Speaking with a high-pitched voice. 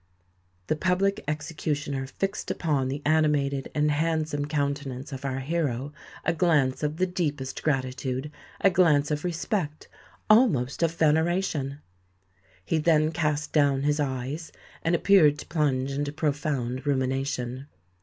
No: medium, 150 Hz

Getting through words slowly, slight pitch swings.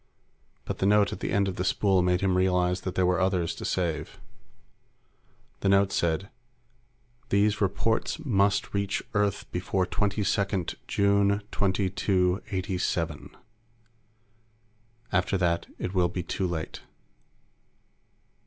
Yes: slow, 120 wpm; narrow, 1.9 semitones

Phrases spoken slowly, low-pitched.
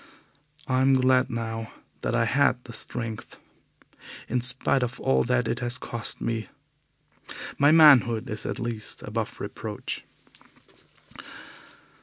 Yes: slow, 125 wpm; low, 120 Hz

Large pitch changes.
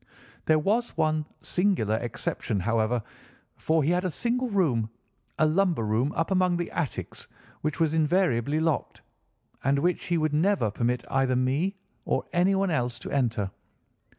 Yes: wide, 6.6 semitones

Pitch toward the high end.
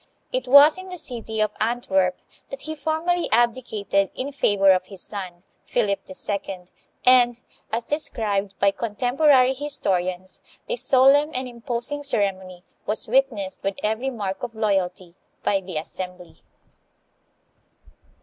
Yes: high, 220 Hz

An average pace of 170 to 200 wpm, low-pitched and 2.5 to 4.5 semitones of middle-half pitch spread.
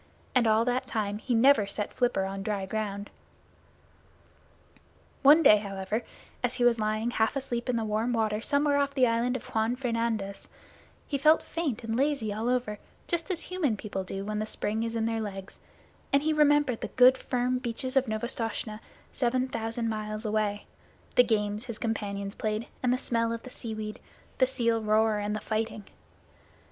No: average, 175 wpm; high, 230 Hz; average, 3.0 semitones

